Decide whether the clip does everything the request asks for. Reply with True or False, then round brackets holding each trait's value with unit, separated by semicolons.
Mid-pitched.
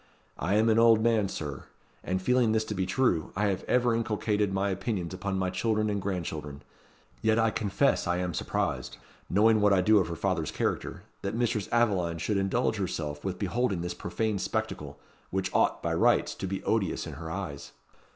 False (100 Hz)